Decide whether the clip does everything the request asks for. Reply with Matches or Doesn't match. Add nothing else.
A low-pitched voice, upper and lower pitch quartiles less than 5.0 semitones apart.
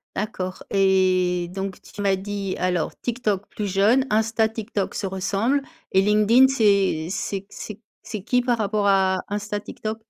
Doesn't match